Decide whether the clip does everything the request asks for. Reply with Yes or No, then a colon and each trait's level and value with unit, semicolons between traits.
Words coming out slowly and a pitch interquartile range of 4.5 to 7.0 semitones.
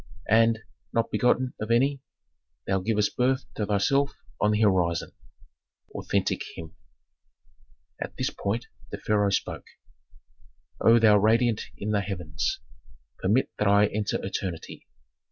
No: slow, 130 wpm; narrow, 2.6 semitones